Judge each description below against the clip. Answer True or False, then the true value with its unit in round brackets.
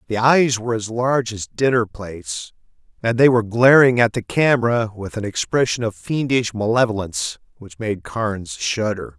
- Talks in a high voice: False (115 Hz)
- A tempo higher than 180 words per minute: False (165 wpm)